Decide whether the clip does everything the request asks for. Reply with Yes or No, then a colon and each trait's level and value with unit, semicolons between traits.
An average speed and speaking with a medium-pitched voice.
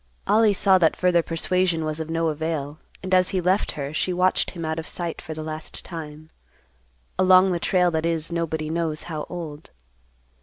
Yes: average, 185 wpm; medium, 165 Hz